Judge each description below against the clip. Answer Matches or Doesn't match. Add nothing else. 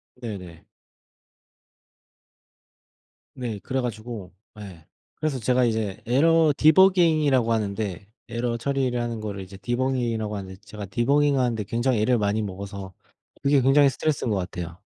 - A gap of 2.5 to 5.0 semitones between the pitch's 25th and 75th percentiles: Matches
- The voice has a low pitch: Matches